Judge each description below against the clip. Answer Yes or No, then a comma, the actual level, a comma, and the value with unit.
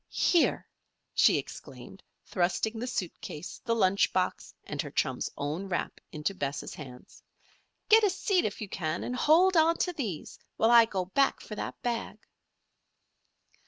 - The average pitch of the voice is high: Yes, high, 210 Hz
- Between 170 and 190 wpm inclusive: No, average, 160 wpm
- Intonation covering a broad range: Yes, wide, 7.6 semitones